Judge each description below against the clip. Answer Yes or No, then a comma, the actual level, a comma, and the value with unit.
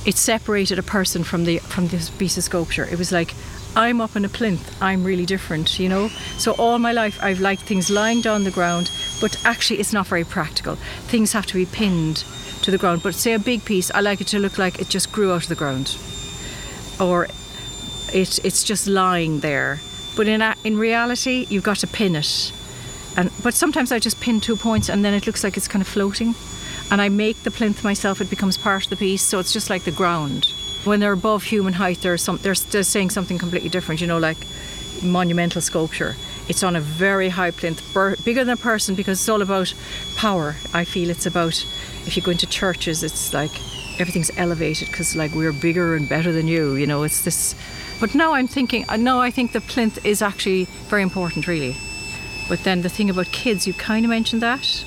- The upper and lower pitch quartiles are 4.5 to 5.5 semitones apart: No, average, 3.7 semitones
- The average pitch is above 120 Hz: Yes, high, 190 Hz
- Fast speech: Yes, fast, 220 wpm